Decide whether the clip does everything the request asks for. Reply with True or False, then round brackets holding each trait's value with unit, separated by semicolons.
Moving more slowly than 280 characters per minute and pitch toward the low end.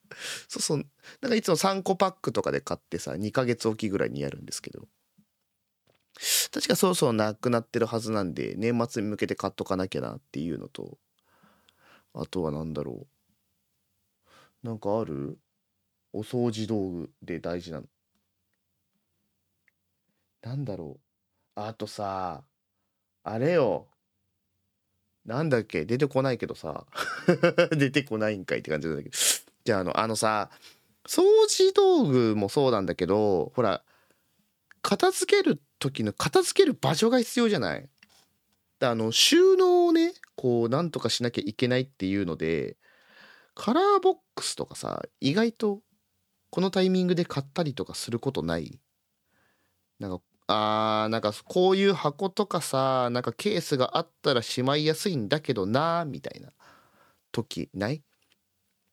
True (265 characters per minute; 115 Hz)